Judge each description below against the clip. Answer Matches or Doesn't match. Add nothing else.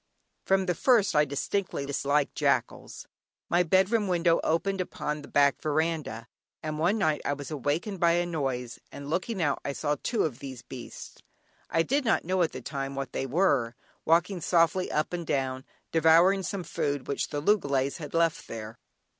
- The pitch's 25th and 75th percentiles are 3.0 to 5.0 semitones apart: Matches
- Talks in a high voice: Doesn't match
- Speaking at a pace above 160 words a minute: Matches